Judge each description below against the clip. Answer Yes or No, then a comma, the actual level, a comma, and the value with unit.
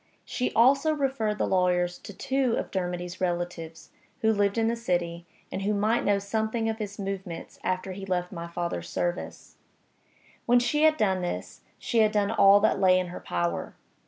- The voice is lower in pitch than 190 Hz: No, high, 195 Hz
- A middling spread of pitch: Yes, average, 3.9 semitones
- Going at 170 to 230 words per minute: Yes, average, 185 wpm